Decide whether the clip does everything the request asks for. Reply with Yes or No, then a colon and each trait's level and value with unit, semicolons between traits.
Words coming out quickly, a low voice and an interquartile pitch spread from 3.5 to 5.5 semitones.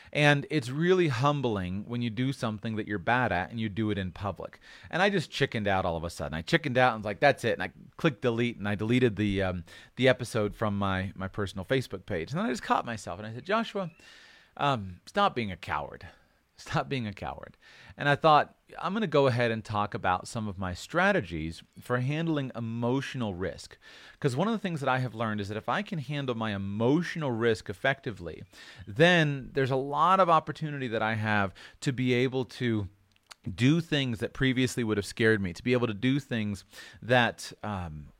Yes: fast, 215 wpm; low, 120 Hz; average, 5.2 semitones